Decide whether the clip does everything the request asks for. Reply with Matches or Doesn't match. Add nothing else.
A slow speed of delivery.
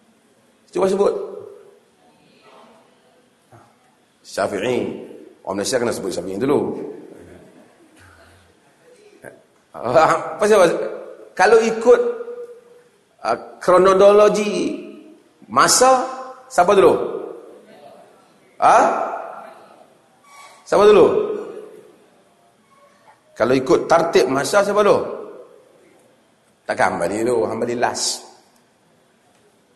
Matches